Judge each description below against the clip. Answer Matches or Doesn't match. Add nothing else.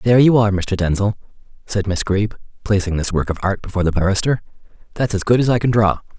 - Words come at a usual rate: Doesn't match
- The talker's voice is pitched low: Matches